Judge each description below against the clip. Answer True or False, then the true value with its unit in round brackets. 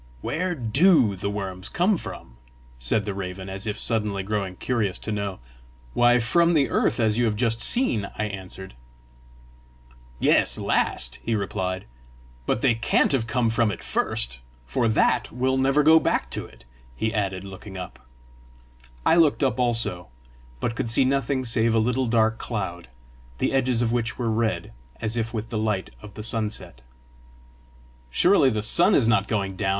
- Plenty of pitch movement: False (4.0 semitones)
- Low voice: True (110 Hz)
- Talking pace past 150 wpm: True (170 wpm)